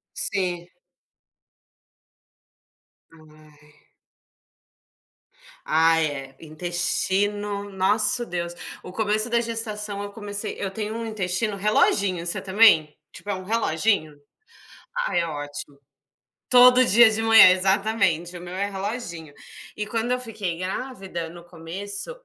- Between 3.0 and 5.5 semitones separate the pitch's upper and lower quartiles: Yes, average, 4.1 semitones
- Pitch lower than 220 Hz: Yes, high, 195 Hz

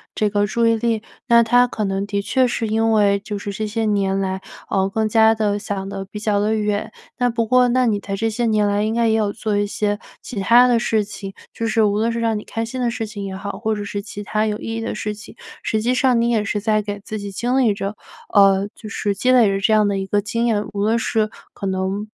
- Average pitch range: No, narrow, 2.0 semitones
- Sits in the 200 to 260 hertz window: Yes, high, 215 Hz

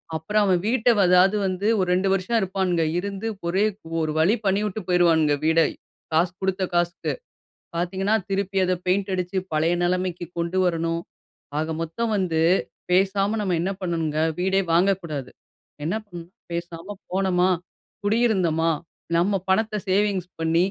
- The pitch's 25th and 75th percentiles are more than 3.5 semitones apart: No, narrow, 2.6 semitones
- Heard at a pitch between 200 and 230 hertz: No, medium, 185 Hz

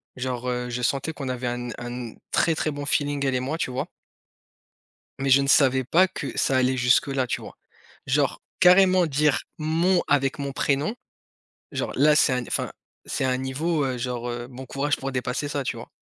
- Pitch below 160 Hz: Yes, low, 135 Hz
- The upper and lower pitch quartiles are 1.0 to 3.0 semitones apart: Yes, narrow, 2.6 semitones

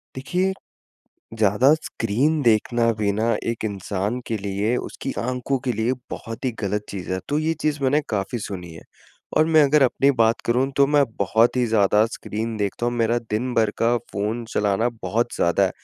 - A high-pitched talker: No, low, 115 Hz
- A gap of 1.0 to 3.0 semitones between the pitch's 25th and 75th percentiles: No, average, 3.8 semitones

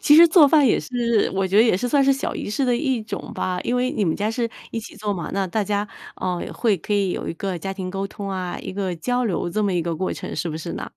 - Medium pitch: No, high, 205 Hz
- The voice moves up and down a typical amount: Yes, average, 4.5 semitones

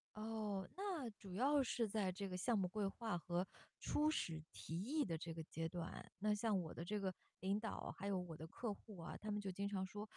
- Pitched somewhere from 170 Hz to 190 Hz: No, high, 200 Hz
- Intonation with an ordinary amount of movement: Yes, average, 3.4 semitones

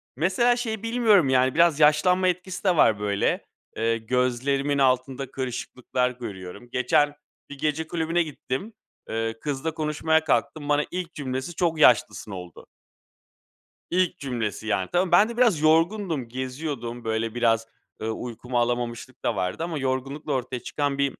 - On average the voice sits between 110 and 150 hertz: Yes, low, 135 Hz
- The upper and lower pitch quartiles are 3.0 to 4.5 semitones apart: No, average, 5.1 semitones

